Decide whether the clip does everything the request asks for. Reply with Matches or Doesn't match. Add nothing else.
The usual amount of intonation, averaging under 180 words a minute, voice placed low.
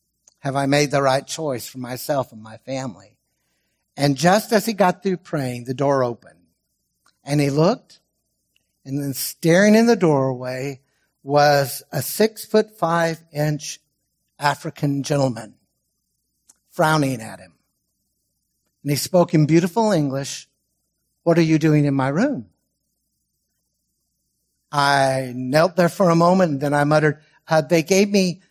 Doesn't match